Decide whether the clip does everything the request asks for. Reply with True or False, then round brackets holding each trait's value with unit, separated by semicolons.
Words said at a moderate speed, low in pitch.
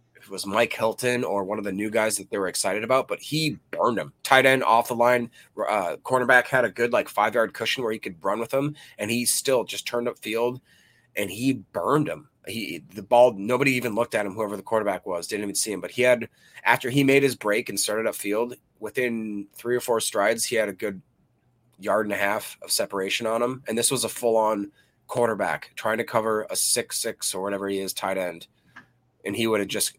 False (235 wpm; 115 Hz)